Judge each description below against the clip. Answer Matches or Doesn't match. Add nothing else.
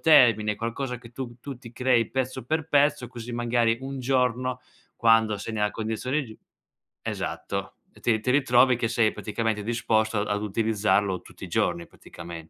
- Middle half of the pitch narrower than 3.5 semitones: Matches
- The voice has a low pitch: Matches